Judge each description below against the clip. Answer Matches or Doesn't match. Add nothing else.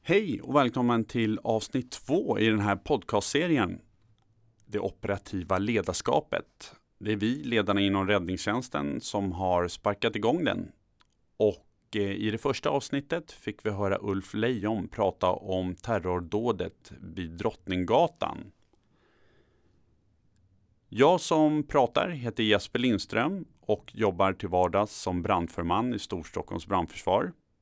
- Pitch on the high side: Doesn't match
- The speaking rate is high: Doesn't match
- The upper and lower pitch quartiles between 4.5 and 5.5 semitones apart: Doesn't match